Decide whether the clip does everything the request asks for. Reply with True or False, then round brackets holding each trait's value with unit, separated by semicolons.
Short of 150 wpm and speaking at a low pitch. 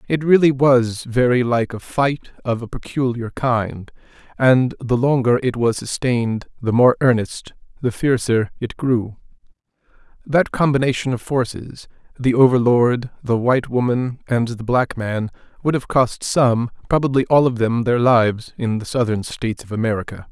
True (140 wpm; 120 Hz)